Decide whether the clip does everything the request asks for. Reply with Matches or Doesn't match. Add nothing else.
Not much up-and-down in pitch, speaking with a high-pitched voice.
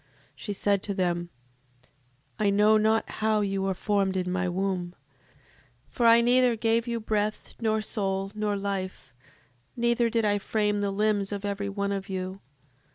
Matches